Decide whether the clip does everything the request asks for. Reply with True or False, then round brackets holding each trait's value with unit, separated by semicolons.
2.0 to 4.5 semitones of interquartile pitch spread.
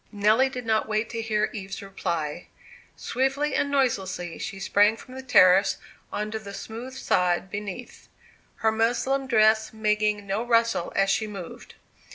True (3.1 semitones)